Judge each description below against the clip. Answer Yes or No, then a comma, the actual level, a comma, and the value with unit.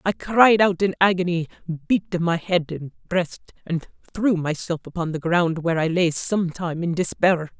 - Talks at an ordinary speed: Yes, average, 180 wpm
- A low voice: No, medium, 175 Hz